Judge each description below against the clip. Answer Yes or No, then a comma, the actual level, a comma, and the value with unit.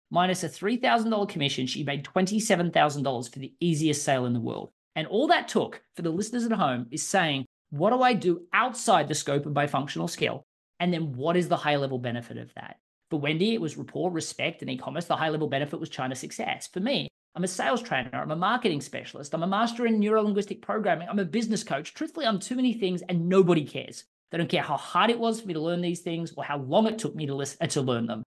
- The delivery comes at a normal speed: No, fast, 245 wpm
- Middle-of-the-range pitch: Yes, medium, 170 Hz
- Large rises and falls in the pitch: Yes, wide, 5.9 semitones